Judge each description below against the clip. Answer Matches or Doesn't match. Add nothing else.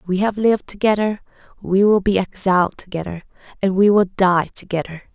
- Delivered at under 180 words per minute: Matches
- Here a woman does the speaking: Matches